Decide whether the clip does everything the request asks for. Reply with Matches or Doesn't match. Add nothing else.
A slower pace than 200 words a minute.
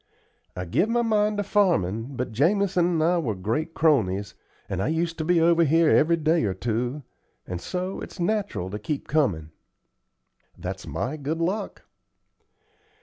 Matches